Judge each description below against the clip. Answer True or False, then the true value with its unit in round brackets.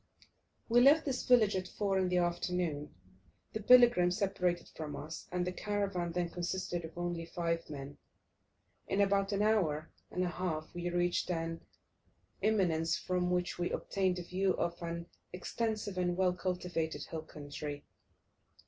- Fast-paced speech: False (155 wpm)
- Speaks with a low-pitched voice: False (180 Hz)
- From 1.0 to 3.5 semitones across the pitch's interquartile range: True (2.5 semitones)